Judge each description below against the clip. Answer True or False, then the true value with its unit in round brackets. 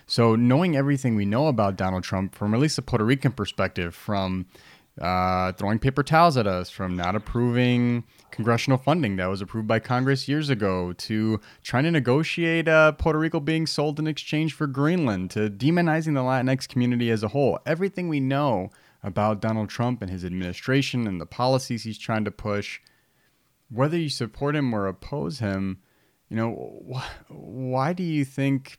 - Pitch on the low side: True (120 Hz)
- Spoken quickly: False (175 wpm)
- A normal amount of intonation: False (5.9 semitones)